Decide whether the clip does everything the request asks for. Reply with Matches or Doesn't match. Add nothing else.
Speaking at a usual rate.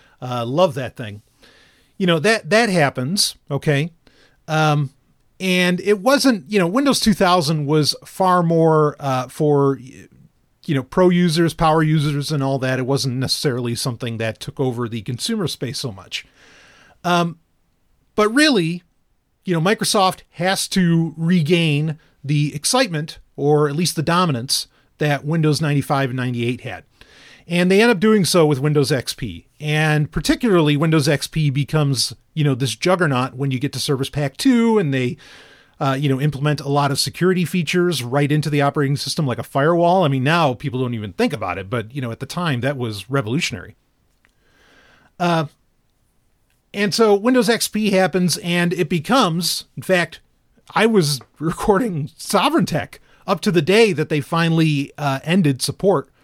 Matches